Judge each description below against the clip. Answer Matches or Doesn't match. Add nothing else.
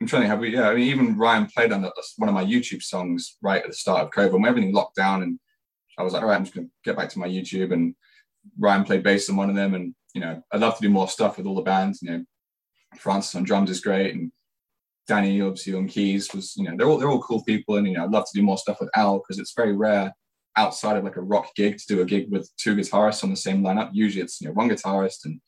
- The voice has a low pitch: Matches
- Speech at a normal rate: Doesn't match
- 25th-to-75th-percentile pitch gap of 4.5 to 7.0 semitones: Doesn't match